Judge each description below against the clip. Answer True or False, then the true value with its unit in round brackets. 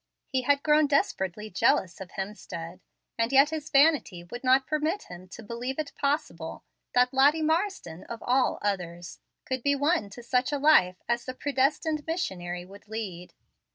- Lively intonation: True (7.2 semitones)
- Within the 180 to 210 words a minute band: False (165 wpm)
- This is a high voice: True (250 Hz)